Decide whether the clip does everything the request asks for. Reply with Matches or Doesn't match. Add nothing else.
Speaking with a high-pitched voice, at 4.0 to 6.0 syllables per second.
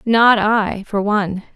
Doesn't match